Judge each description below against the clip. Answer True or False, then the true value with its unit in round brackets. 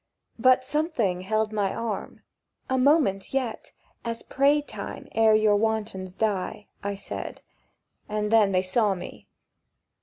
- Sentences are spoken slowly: True (130 wpm)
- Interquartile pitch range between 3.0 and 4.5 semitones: True (3.7 semitones)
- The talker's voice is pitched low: False (215 Hz)